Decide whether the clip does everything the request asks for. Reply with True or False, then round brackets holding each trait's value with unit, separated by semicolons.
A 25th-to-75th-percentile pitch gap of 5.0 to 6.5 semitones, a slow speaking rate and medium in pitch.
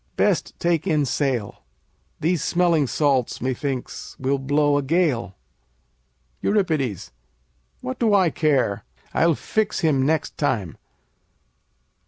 False (4.2 semitones; 110 wpm; 145 Hz)